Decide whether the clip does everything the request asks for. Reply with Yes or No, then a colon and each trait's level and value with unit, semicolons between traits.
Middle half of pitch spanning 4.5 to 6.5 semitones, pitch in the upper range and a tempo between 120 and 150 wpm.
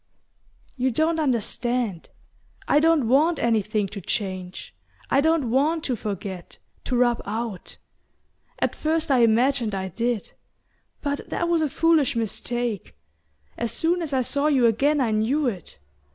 Yes: average, 5.3 semitones; high, 245 Hz; average, 145 wpm